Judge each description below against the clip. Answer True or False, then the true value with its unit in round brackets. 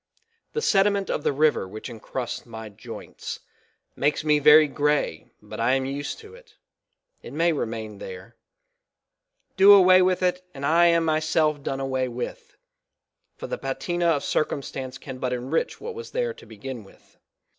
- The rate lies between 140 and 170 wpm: True (165 wpm)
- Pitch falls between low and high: True (150 Hz)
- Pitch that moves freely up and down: True (5.9 semitones)